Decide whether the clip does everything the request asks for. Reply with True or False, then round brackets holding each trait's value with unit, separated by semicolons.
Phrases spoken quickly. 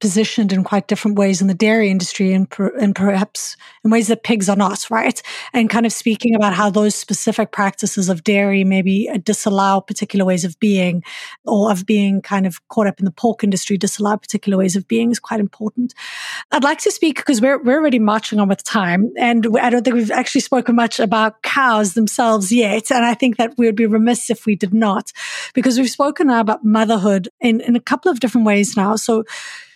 True (215 wpm)